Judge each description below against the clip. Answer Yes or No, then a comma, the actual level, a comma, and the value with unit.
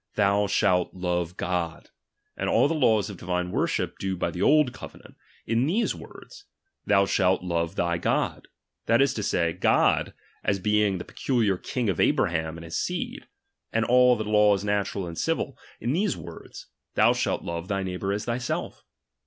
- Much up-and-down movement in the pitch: No, average, 4.1 semitones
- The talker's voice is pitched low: Yes, low, 100 Hz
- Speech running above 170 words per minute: Yes, average, 180 wpm